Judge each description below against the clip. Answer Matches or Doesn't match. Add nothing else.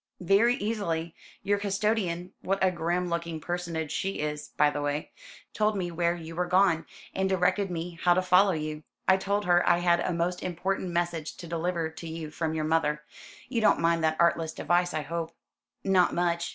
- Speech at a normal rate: Matches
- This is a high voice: Doesn't match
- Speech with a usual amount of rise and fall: Doesn't match